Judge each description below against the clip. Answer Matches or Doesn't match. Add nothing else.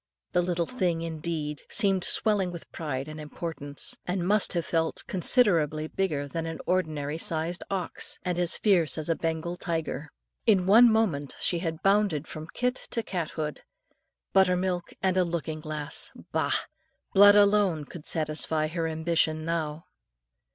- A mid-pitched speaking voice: Matches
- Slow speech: Doesn't match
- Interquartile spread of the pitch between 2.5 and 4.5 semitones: Matches